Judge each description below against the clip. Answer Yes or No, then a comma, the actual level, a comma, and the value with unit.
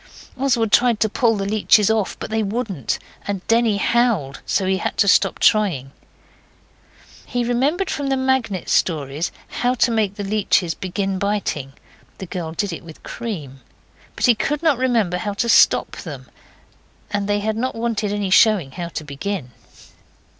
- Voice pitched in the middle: No, high, 205 Hz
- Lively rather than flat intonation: No, average, 4.2 semitones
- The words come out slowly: No, average, 170 wpm